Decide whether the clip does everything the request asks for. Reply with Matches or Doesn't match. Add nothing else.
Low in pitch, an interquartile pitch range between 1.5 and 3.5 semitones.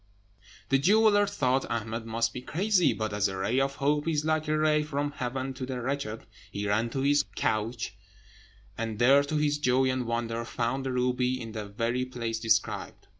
Doesn't match